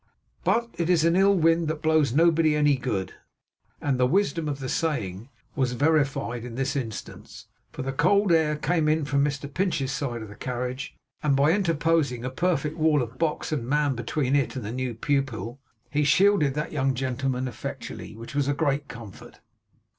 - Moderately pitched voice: Yes, medium, 145 Hz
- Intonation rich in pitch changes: No, average, 3.7 semitones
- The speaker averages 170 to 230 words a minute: Yes, average, 185 wpm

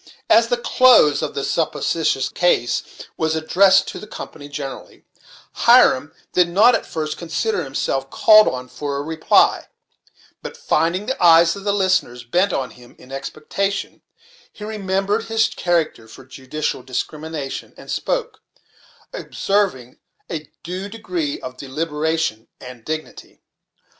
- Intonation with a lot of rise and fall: Yes, wide, 6.1 semitones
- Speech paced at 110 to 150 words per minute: Yes, slow, 135 wpm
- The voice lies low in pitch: No, medium, 160 Hz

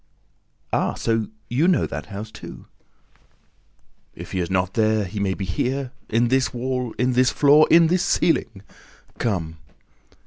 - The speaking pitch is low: Yes, low, 115 Hz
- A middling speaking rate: Yes, average, 150 wpm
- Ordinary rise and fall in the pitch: Yes, average, 4.8 semitones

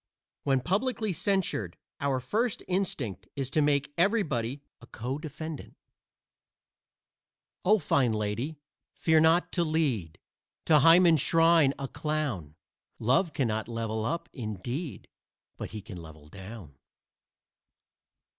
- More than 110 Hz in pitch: Yes, medium, 140 Hz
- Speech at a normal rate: No, slow, 110 wpm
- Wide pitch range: Yes, wide, 6.8 semitones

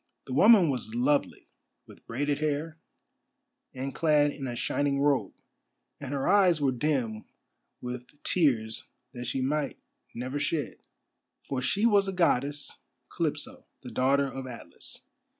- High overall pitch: No, medium, 140 Hz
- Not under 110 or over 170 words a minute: Yes, slow, 135 wpm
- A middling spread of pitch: Yes, average, 3.0 semitones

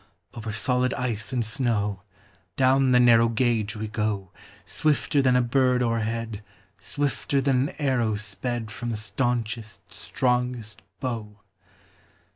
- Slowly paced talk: Yes, slow, 125 wpm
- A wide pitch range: No, average, 2.7 semitones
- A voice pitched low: Yes, low, 120 Hz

